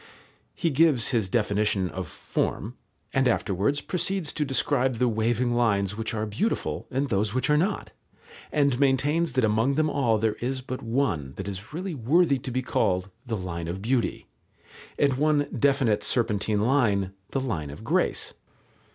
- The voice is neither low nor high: No, low, 120 Hz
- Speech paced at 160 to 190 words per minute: Yes, average, 165 wpm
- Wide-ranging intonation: No, average, 5.0 semitones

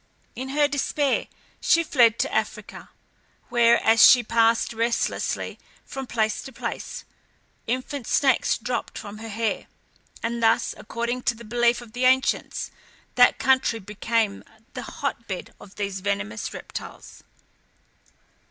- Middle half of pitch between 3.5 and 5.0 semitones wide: No, narrow, 2.6 semitones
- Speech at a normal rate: No, slow, 130 wpm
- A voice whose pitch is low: No, high, 235 Hz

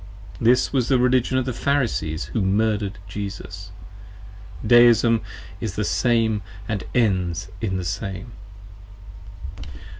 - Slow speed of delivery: Yes, slow, 115 wpm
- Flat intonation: No, average, 3.7 semitones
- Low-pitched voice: Yes, low, 110 Hz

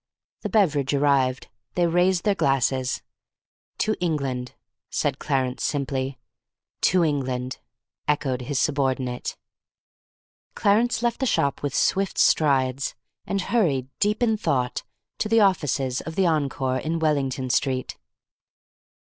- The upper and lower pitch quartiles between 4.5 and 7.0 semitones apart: Yes, wide, 5.5 semitones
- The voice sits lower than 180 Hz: Yes, medium, 140 Hz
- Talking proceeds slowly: Yes, slow, 120 wpm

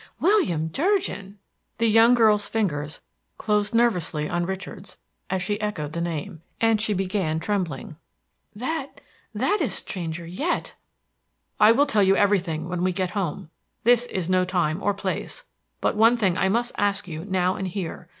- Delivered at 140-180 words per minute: Yes, average, 160 wpm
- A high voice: Yes, high, 195 Hz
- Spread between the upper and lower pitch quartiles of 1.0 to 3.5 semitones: No, average, 4.2 semitones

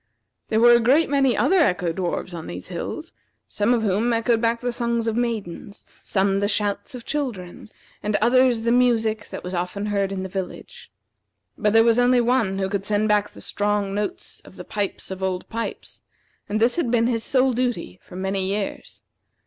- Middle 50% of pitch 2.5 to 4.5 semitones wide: Yes, average, 3.5 semitones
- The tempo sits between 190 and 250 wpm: Yes, average, 195 wpm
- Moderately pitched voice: No, high, 215 Hz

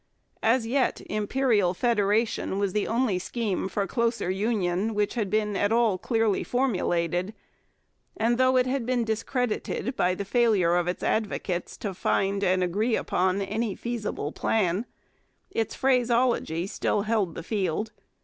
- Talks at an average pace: Yes, average, 145 wpm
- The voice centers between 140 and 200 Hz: No, high, 210 Hz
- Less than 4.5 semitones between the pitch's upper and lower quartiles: Yes, average, 3.8 semitones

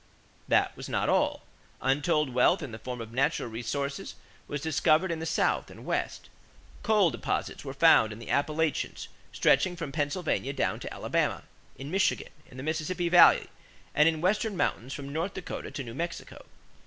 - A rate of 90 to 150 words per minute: No, average, 175 wpm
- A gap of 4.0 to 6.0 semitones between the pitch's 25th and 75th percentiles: Yes, average, 4.3 semitones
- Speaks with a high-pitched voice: No, medium, 150 Hz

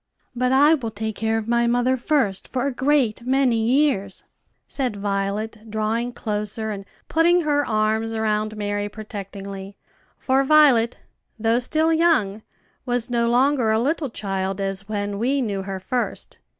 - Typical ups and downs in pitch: Yes, average, 4.0 semitones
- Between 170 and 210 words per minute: No, average, 150 wpm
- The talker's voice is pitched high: Yes, high, 225 Hz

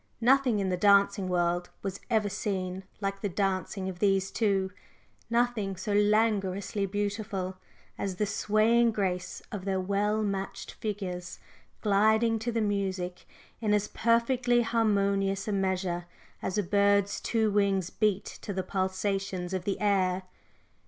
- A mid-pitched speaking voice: No, high, 200 Hz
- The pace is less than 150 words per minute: Yes, average, 140 wpm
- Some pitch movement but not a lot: No, narrow, 2.1 semitones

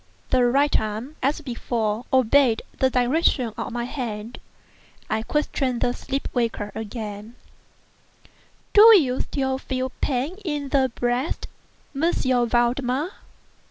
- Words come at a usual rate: No, slow, 120 wpm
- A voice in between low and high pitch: No, very high, 255 Hz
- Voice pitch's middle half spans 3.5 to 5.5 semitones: No, average, 2.8 semitones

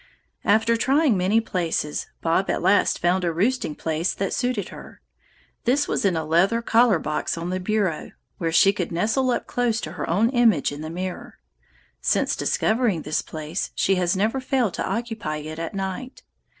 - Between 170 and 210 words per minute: Yes, average, 180 wpm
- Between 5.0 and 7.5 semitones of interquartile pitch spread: Yes, wide, 5.5 semitones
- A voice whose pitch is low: No, high, 190 Hz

